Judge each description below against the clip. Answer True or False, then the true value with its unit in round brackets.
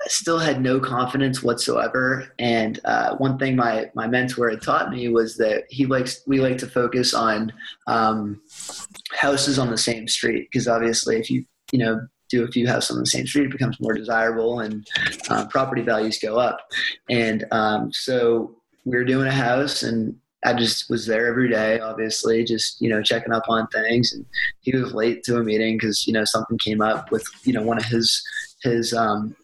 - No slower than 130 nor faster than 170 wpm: False (200 wpm)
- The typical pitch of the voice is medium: False (115 Hz)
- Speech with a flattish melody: True (2.3 semitones)